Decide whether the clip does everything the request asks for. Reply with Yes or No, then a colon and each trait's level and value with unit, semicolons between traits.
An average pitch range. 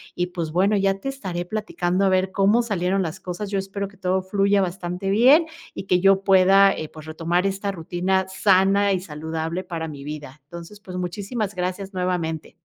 No: narrow, 2.1 semitones